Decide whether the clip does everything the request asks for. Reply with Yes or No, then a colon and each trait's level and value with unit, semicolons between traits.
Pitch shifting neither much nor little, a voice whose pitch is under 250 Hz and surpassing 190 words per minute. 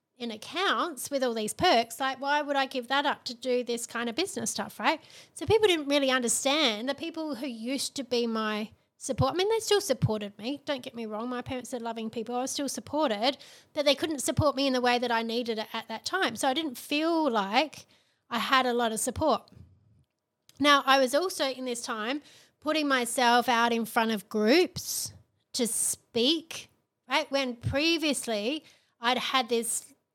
No: average, 3.6 semitones; very high, 260 Hz; average, 200 wpm